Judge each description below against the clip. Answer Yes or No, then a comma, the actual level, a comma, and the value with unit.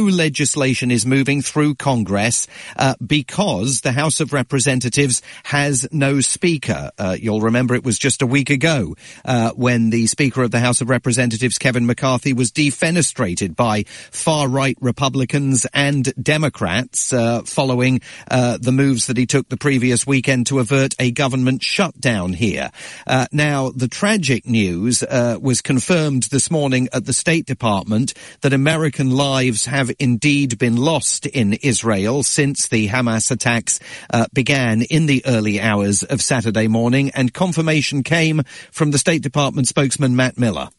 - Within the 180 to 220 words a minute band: No, average, 155 wpm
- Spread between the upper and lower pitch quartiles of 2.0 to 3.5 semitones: Yes, average, 2.8 semitones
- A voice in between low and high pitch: No, low, 130 Hz